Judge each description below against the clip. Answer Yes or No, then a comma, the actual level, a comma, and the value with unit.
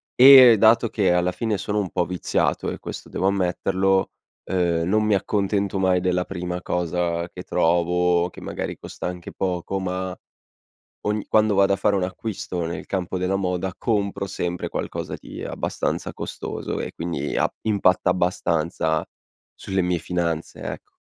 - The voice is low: Yes, very low, 90 Hz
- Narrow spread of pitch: Yes, narrow, 2.0 semitones